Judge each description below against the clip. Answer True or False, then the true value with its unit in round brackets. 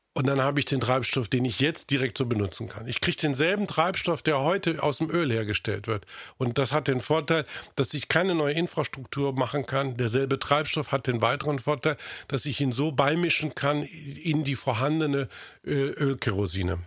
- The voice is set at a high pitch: False (140 Hz)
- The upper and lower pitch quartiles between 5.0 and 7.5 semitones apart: False (3.0 semitones)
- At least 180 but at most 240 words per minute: True (185 wpm)